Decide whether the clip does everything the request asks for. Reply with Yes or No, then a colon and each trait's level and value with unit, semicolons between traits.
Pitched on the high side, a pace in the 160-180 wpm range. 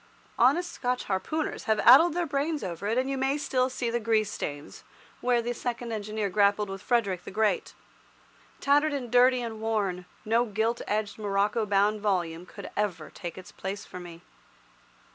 Yes: high, 220 Hz; average, 175 wpm